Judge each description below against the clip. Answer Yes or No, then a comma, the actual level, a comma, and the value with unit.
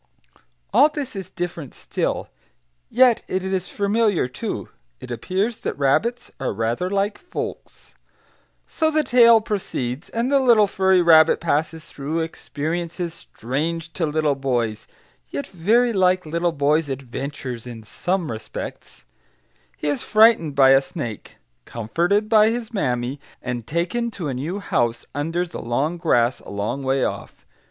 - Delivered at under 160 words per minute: Yes, average, 145 wpm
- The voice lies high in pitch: No, medium, 165 Hz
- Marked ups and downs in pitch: Yes, wide, 6.9 semitones